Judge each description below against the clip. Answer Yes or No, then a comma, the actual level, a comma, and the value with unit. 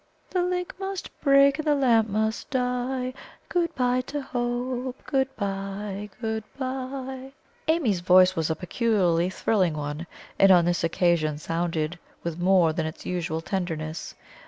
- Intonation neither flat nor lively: No, wide, 7.0 semitones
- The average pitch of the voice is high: Yes, high, 210 Hz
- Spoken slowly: No, average, 145 wpm